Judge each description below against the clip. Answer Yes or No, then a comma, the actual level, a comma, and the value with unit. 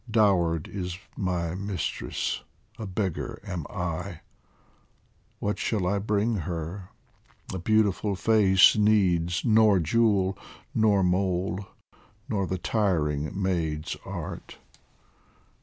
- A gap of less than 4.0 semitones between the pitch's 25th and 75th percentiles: Yes, average, 2.9 semitones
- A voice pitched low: Yes, very low, 95 Hz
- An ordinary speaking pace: No, slow, 100 wpm